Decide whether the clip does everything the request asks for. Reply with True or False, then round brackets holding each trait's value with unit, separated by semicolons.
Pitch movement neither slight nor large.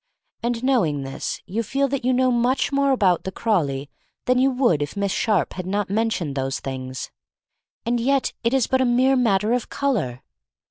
False (6.6 semitones)